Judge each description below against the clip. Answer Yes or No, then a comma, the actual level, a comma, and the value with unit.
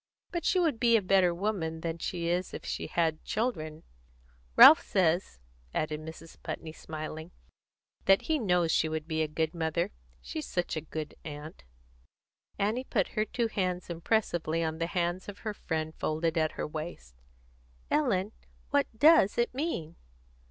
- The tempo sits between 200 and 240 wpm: No, average, 160 wpm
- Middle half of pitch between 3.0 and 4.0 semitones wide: No, average, 4.5 semitones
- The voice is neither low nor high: Yes, medium, 170 Hz